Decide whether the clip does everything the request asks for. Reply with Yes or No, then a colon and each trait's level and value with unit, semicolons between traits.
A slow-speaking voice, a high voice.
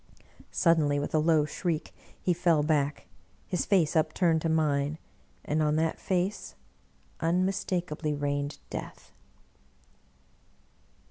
No: slow, 110 wpm; medium, 160 Hz